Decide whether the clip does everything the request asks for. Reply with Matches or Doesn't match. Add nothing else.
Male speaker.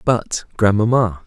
Matches